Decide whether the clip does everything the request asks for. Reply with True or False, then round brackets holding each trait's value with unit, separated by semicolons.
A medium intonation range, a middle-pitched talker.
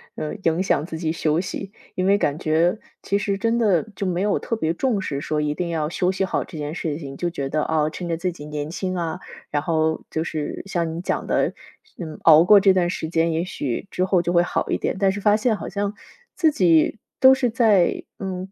True (3.6 semitones; 175 Hz)